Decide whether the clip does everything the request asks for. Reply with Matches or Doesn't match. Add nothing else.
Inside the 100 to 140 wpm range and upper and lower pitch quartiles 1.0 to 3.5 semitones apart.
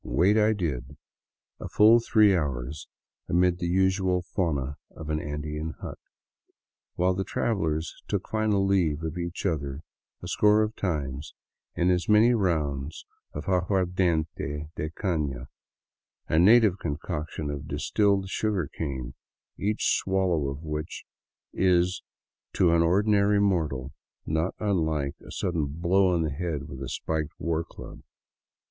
Doesn't match